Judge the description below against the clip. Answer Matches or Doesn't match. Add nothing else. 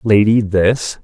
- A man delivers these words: Matches